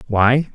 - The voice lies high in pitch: No, low, 120 Hz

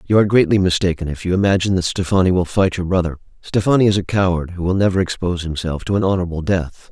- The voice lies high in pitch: No, very low, 90 Hz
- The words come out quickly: Yes, fast, 225 wpm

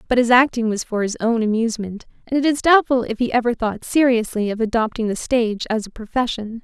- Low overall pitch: No, high, 230 Hz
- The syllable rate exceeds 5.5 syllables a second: Yes, 6.0 syllables/s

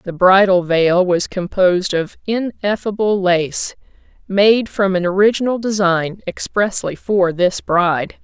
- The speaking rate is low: Yes, slow, 125 wpm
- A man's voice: No, female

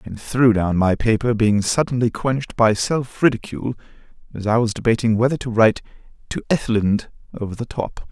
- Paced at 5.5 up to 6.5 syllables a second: Yes, 5.6 syllables/s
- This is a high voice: No, low, 115 Hz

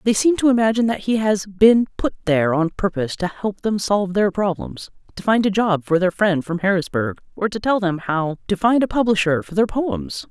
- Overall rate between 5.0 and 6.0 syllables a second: Yes, 5.4 syllables/s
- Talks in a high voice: Yes, high, 195 Hz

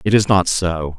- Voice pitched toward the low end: Yes, very low, 90 Hz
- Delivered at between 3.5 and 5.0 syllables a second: Yes, 4.5 syllables/s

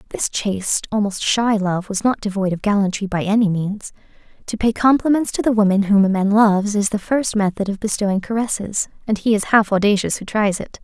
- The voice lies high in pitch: Yes, high, 205 Hz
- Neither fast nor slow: No, fast, 210 wpm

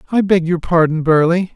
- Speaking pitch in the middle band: Yes, medium, 170 Hz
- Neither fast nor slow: Yes, average, 195 wpm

